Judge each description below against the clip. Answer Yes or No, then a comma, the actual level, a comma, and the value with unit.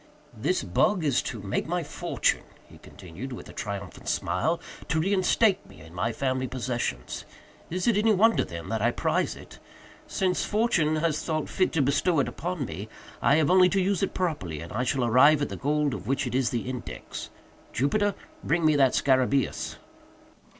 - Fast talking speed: No, average, 185 wpm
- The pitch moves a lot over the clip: Yes, wide, 6.9 semitones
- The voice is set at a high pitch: No, medium, 140 Hz